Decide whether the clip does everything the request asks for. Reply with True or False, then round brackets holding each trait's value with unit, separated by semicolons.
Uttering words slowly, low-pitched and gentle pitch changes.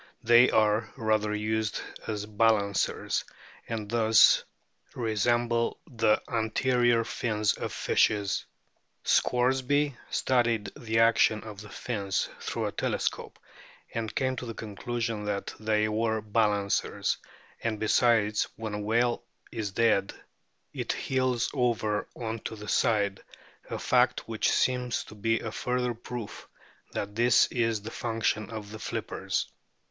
True (130 wpm; 110 Hz; 2.0 semitones)